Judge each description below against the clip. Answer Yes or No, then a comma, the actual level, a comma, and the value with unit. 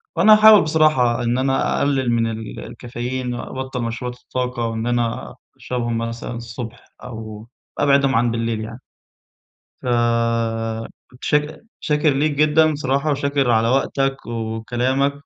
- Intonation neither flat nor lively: Yes, average, 3.0 semitones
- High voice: No, low, 125 Hz